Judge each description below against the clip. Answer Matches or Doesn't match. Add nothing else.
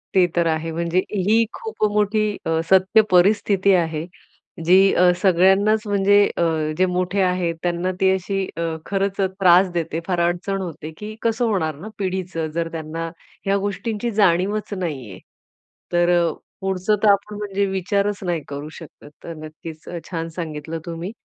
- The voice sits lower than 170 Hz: Doesn't match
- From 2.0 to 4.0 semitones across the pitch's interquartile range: Matches